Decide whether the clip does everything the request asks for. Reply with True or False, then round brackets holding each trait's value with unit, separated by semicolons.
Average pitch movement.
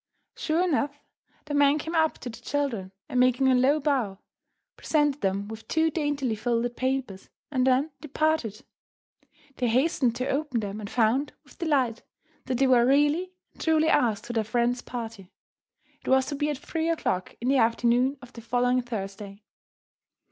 True (4.1 semitones)